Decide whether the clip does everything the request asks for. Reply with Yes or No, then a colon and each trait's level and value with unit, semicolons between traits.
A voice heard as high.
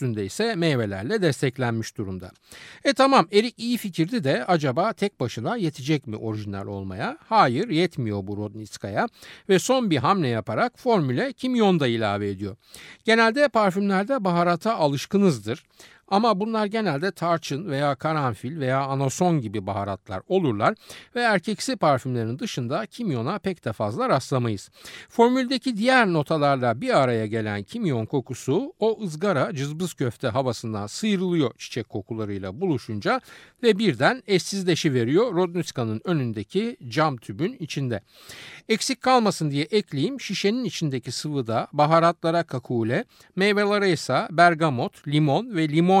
No: medium, 155 Hz